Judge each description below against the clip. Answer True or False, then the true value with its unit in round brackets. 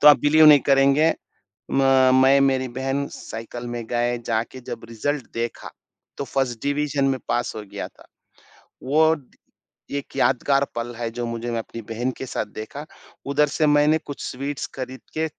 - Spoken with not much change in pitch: False (3.3 semitones)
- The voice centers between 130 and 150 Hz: True (135 Hz)